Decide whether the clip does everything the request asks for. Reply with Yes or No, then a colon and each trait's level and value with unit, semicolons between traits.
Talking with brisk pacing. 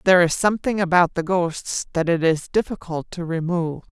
No: average, 180 wpm